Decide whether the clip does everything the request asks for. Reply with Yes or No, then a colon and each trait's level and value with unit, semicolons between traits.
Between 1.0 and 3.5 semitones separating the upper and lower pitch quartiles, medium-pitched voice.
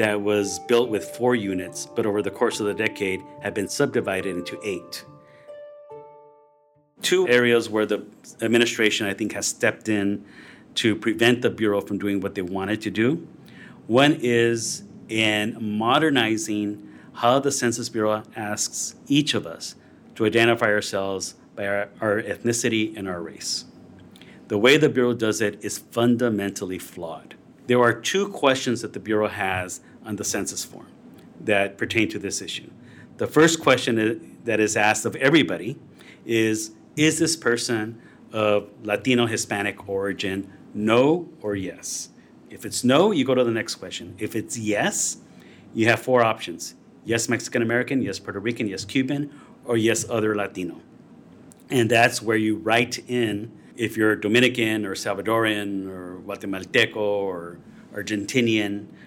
No: average, 2.8 semitones; low, 110 Hz